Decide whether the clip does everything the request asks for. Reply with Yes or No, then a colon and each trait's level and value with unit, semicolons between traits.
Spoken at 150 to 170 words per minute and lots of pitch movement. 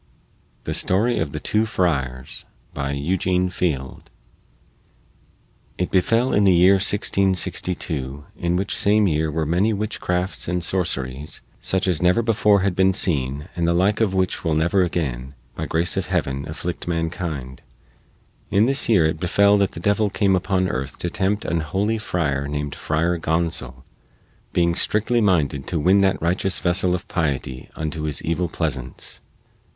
No: average, 155 wpm; average, 4.0 semitones